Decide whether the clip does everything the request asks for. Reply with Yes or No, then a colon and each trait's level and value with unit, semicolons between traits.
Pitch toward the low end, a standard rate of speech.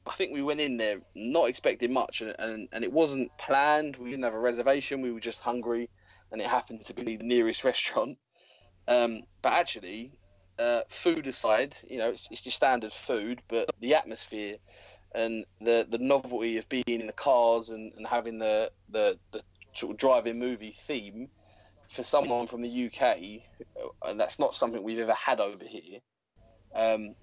Yes: low, 115 Hz; average, 185 wpm